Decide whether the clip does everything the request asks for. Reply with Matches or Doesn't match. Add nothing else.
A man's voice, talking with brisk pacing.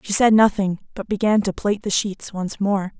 Doesn't match